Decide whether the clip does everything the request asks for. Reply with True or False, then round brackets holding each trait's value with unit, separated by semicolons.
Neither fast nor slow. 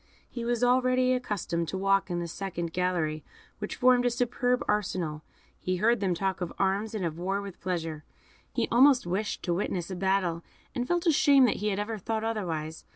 True (190 wpm)